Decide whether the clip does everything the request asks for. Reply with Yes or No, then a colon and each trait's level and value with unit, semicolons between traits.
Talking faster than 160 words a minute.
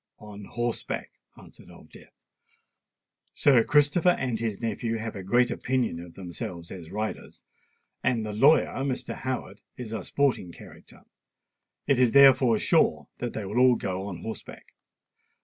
No: average, 150 wpm